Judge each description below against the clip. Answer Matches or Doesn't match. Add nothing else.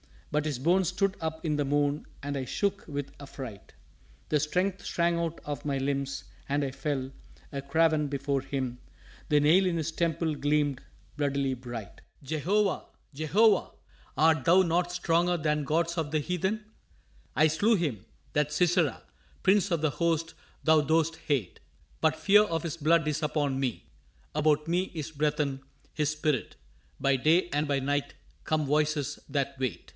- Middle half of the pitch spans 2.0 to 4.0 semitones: Matches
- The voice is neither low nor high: Matches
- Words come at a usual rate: Matches